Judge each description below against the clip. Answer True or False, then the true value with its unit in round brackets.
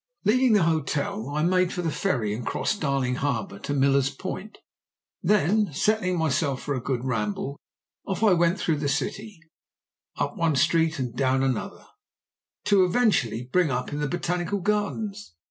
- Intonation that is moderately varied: False (6.2 semitones)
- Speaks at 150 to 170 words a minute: True (165 wpm)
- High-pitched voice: False (160 Hz)